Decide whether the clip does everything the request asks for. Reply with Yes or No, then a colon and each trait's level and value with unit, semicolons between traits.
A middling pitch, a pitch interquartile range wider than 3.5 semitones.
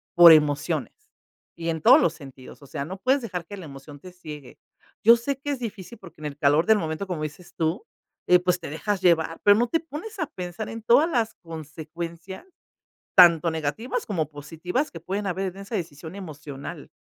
Yes: medium, 175 Hz; average, 4.9 semitones